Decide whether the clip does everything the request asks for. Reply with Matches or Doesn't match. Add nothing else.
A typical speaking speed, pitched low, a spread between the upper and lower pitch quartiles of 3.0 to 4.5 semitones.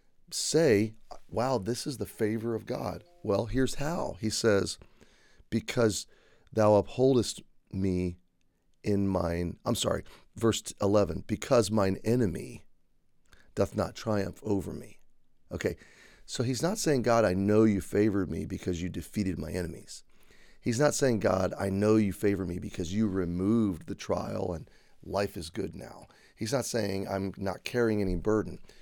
Matches